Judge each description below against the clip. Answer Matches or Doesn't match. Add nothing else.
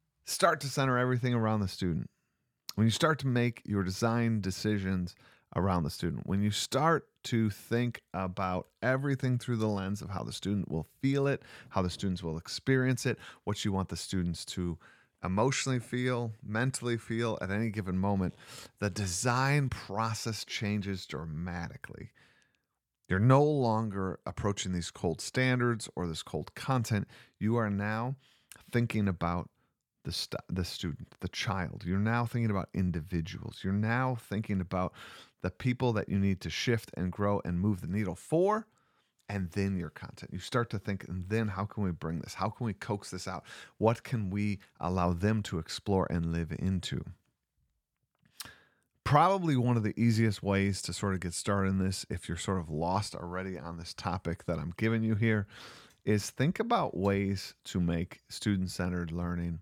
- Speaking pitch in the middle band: Doesn't match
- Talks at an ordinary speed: Matches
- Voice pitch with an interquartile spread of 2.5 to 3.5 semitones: Doesn't match